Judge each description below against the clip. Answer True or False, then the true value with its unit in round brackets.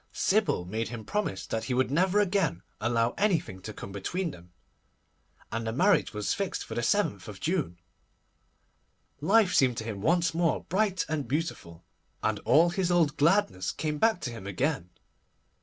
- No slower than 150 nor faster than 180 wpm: True (165 wpm)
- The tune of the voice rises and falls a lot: True (8.8 semitones)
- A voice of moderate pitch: True (145 Hz)